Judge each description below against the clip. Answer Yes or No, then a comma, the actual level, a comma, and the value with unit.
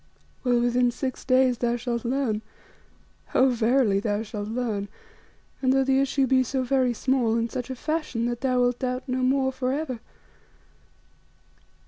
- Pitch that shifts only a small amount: Yes, narrow, 1.9 semitones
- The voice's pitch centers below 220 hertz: No, very high, 250 Hz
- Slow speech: No, average, 160 wpm